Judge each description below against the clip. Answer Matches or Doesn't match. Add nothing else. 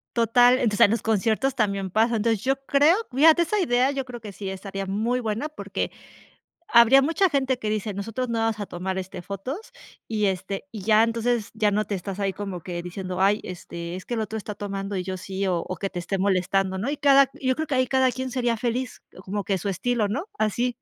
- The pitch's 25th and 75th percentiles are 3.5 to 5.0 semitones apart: Matches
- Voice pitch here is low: Doesn't match